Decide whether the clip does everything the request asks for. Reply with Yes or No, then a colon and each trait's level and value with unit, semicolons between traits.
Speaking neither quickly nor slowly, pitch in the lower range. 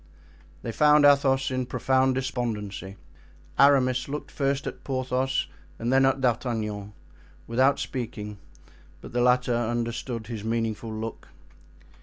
No: slow, 120 wpm; low, 125 Hz